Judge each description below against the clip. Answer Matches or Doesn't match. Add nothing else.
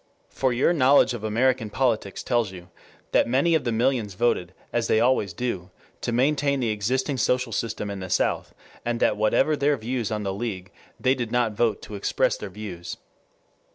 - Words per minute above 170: Matches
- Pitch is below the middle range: Matches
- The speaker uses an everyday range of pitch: Matches